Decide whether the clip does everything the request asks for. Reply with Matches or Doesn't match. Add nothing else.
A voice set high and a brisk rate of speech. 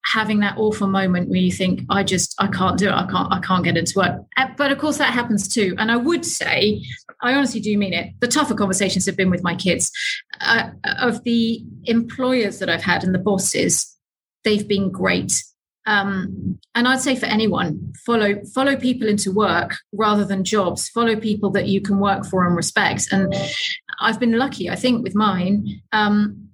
Matches